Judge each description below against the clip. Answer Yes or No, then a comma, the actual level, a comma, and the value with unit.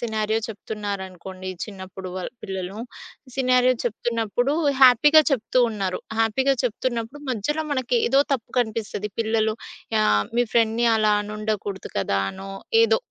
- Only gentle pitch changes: No, average, 3.3 semitones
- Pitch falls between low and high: No, high, 220 Hz